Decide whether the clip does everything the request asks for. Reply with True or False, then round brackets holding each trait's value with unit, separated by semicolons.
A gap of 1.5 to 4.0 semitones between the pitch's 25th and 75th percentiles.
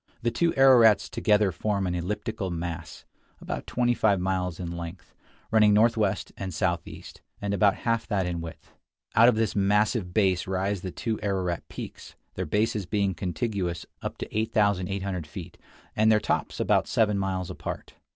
True (3.2 semitones)